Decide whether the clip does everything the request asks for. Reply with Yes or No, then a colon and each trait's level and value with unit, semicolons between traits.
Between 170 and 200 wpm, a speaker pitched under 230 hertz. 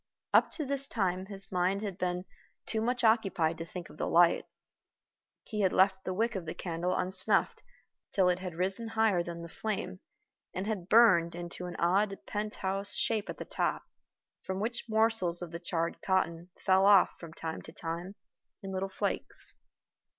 Yes: average, 180 wpm; high, 190 Hz